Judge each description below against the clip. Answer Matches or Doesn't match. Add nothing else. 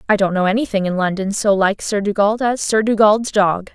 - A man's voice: Doesn't match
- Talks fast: Matches